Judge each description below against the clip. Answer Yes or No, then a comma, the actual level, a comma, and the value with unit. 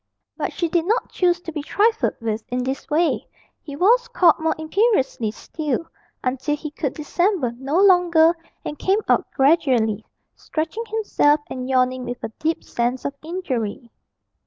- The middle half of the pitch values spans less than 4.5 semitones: No, wide, 5.6 semitones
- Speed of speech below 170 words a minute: Yes, average, 160 wpm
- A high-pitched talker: Yes, very high, 305 Hz